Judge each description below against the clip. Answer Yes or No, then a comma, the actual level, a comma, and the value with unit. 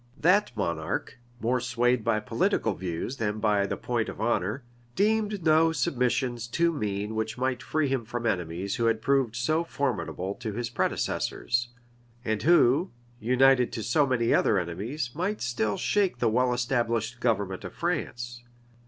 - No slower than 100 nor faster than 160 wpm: Yes, average, 155 wpm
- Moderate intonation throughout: Yes, average, 3.9 semitones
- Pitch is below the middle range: Yes, low, 120 Hz